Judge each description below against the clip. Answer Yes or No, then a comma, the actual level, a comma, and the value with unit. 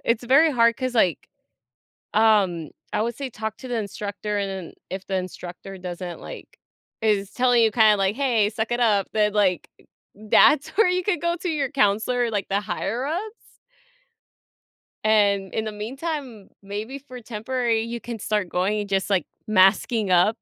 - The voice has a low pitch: No, high, 215 Hz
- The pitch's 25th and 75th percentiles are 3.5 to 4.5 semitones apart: Yes, average, 3.8 semitones